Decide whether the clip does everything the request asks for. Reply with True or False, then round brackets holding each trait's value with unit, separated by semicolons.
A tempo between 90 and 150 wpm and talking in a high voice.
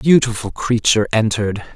False (135 wpm; 110 Hz)